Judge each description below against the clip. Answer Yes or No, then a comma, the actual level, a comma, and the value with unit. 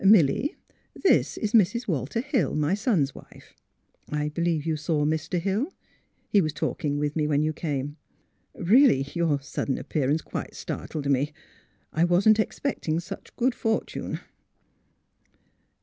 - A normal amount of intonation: No, wide, 5.8 semitones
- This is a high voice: No, medium, 160 Hz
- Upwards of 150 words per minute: No, average, 140 wpm